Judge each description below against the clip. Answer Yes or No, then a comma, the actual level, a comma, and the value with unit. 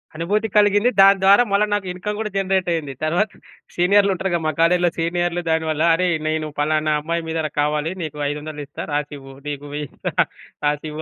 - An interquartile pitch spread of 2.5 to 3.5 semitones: No, average, 4.0 semitones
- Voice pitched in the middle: Yes, medium, 165 Hz